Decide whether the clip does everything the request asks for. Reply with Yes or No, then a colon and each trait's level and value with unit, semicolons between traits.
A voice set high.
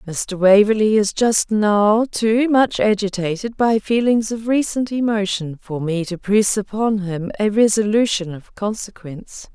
Yes: high, 210 Hz